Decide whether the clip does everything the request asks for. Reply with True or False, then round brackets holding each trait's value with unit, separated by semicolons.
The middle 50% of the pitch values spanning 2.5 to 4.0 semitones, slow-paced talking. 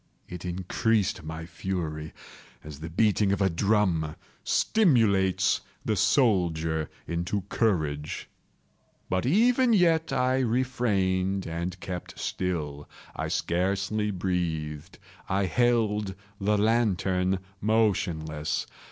False (4.7 semitones; 100 wpm)